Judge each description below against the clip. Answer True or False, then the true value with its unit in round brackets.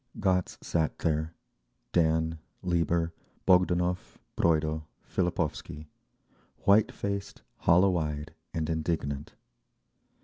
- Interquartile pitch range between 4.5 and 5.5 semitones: False (2.4 semitones)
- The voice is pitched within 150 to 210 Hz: False (80 Hz)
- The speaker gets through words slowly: True (75 wpm)